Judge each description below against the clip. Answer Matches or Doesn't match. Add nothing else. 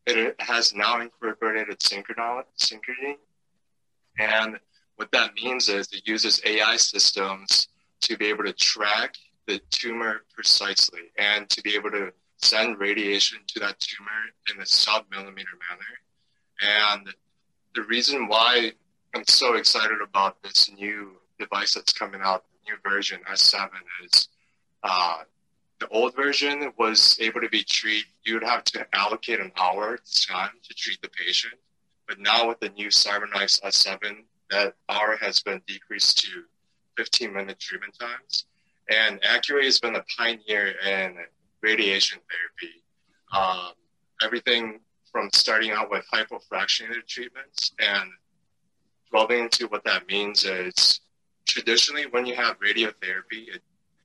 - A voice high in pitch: Doesn't match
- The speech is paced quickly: Doesn't match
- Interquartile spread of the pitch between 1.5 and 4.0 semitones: Matches